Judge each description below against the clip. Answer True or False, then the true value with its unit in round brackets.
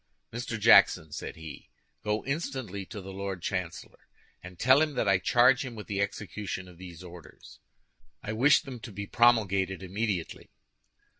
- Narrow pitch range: False (4.3 semitones)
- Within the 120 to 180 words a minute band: True (160 wpm)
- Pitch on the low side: True (100 Hz)